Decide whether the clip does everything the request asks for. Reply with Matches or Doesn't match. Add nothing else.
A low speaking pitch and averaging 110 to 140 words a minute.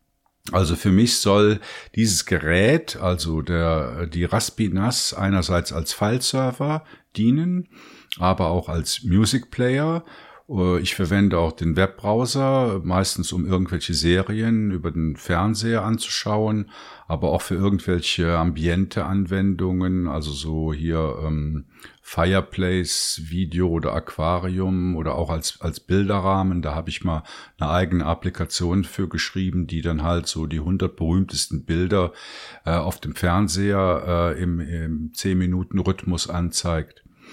Matches